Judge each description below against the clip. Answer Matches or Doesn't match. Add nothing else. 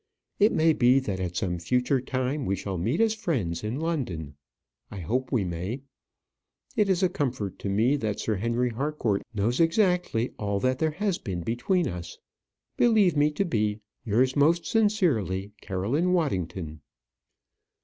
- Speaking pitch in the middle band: Doesn't match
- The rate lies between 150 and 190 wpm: Matches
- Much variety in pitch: Matches